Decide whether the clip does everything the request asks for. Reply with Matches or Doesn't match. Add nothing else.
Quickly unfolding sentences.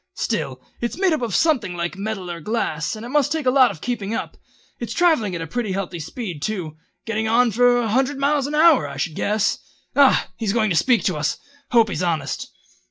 Matches